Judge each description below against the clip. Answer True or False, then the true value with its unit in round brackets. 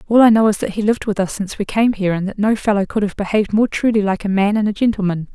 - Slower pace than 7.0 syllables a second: False (7.2 syllables/s)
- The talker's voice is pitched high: True (205 Hz)